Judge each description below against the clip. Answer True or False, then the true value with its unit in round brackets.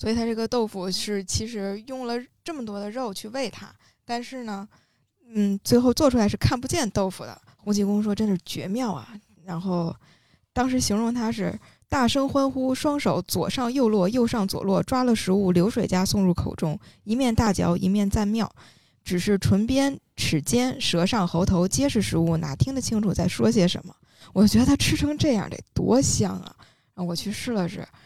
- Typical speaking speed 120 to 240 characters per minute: False (275 characters per minute)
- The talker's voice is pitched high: True (205 Hz)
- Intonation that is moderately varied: True (4.6 semitones)